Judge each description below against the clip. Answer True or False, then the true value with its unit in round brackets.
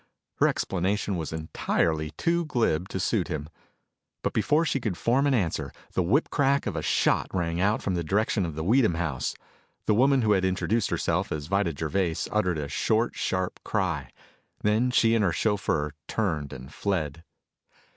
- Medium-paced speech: True (175 wpm)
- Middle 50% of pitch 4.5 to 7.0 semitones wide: True (5.4 semitones)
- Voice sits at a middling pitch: False (95 Hz)